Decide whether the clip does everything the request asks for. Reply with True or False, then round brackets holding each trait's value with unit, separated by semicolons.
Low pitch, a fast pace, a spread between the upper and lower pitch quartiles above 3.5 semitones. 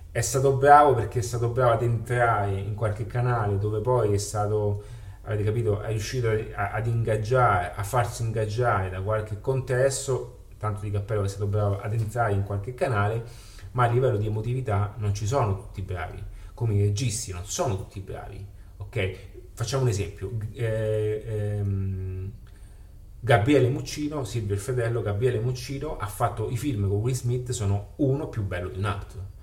False (110 Hz; 175 wpm; 3.2 semitones)